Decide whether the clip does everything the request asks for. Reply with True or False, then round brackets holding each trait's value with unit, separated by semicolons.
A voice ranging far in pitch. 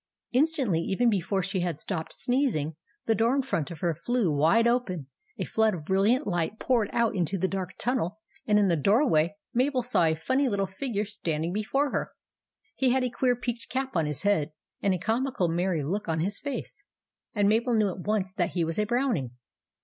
True (6.0 semitones)